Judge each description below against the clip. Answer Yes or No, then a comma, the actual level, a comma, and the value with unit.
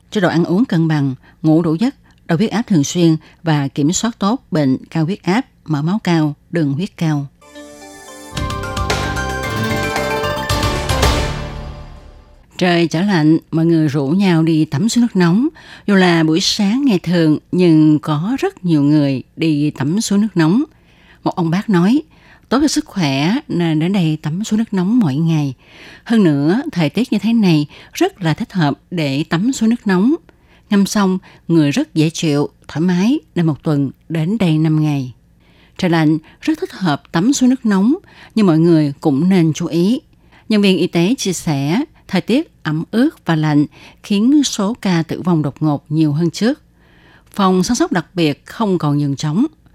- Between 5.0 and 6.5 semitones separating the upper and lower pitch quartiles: Yes, average, 5.3 semitones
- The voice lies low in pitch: No, medium, 165 Hz